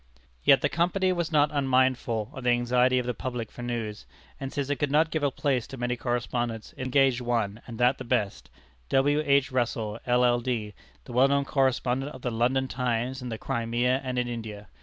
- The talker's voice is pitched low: Yes, low, 125 Hz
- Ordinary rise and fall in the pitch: No, narrow, 2.1 semitones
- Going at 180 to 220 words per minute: Yes, average, 200 wpm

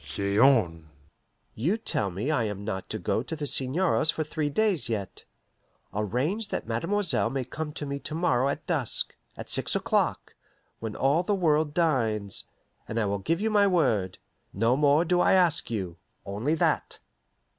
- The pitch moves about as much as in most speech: No, wide, 7.2 semitones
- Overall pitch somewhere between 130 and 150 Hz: Yes, medium, 140 Hz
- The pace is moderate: Yes, average, 170 wpm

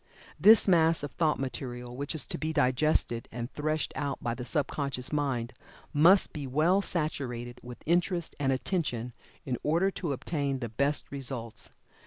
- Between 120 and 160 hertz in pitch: Yes, medium, 140 Hz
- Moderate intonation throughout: Yes, average, 4.1 semitones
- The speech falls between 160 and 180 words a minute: Yes, average, 165 wpm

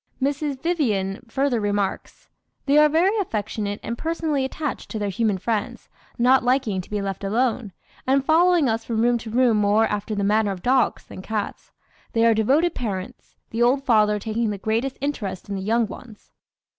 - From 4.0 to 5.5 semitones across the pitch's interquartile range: Yes, average, 4.4 semitones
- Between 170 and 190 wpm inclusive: Yes, average, 180 wpm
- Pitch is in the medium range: No, high, 230 Hz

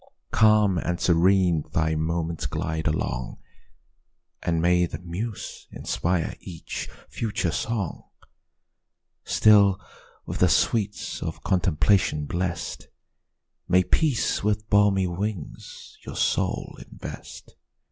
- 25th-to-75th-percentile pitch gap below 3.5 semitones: No, average, 3.8 semitones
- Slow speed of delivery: Yes, slow, 100 wpm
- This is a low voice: Yes, very low, 90 Hz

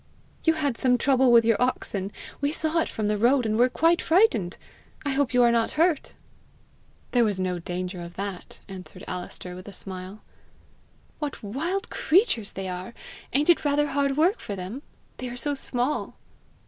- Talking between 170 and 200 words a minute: Yes, average, 180 wpm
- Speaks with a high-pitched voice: Yes, high, 245 Hz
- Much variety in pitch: Yes, wide, 6.8 semitones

